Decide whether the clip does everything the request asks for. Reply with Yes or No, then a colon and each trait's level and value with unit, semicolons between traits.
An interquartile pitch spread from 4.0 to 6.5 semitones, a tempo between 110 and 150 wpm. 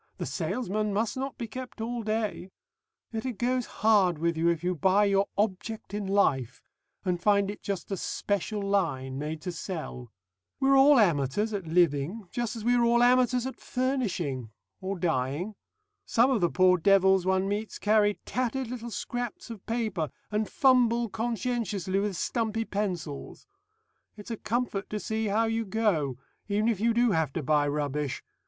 No: average, 4.6 semitones; average, 170 wpm